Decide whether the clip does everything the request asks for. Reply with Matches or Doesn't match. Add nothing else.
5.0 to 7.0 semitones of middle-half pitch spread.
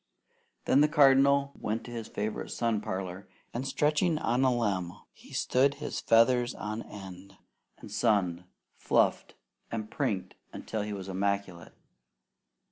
Matches